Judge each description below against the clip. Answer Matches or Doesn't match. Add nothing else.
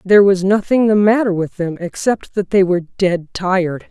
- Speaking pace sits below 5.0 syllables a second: Doesn't match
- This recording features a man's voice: Doesn't match